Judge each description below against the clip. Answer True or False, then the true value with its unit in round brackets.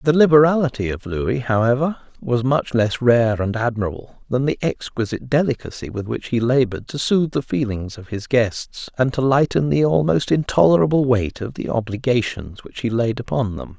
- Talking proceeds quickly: False (180 wpm)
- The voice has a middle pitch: False (125 Hz)